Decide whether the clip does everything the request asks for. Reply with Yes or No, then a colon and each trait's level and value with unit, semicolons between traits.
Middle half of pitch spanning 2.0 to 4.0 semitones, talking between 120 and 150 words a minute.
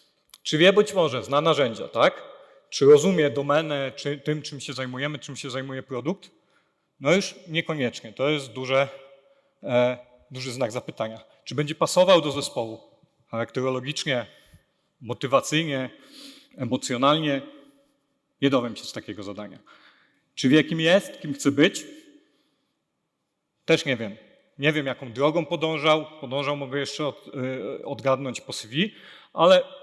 No: average, 4.7 semitones; average, 135 wpm